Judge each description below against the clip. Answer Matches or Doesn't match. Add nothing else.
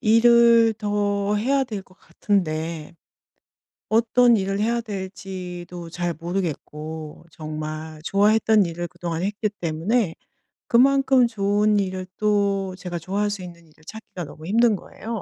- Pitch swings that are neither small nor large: Matches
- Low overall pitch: Doesn't match